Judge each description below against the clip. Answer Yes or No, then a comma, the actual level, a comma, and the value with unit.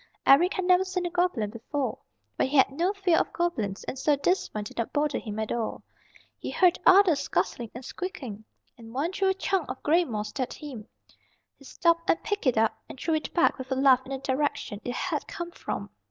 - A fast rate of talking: Yes, fast, 225 wpm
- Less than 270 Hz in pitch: No, very high, 285 Hz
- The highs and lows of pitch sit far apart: Yes, wide, 6.4 semitones